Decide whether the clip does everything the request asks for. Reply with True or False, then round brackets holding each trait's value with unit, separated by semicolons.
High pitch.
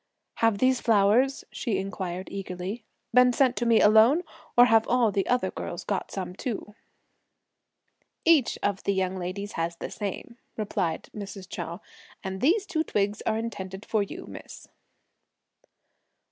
True (205 Hz)